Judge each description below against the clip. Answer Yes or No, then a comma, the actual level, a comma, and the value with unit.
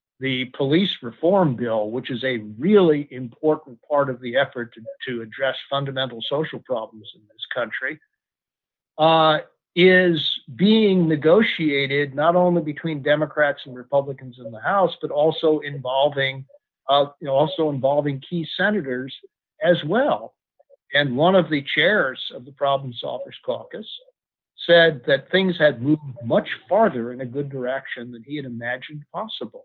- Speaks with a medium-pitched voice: Yes, medium, 145 Hz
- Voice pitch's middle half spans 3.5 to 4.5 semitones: Yes, average, 4.1 semitones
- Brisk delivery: No, average, 150 wpm